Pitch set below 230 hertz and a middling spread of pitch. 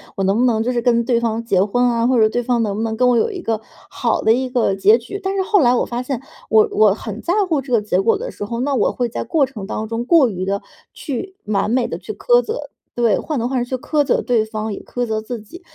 No: high, 240 Hz; average, 3.5 semitones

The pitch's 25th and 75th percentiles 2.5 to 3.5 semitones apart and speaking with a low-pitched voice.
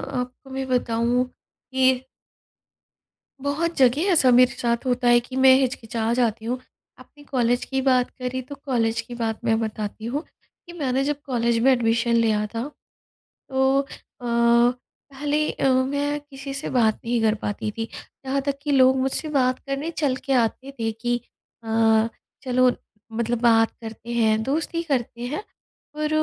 No: average, 2.9 semitones; very high, 250 Hz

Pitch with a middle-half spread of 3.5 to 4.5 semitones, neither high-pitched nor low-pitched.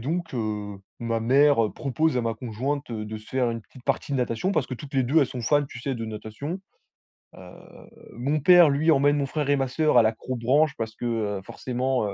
No: average, 4.0 semitones; low, 130 Hz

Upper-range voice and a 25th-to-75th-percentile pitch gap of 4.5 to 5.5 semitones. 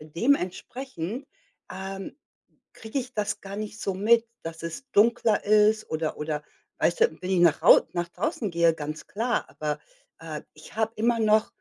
Yes: high, 205 Hz; average, 5.2 semitones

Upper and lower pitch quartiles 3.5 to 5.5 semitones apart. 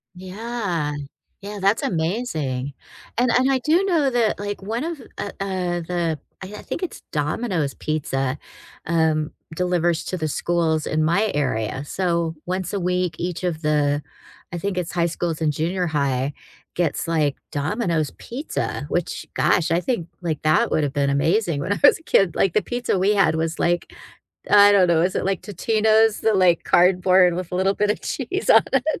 Yes: average, 4.5 semitones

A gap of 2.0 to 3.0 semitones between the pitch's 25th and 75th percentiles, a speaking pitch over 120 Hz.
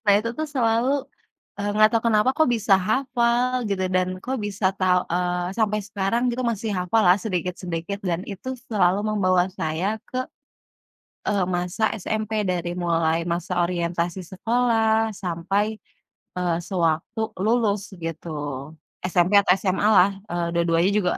No: average, 3.8 semitones; high, 190 Hz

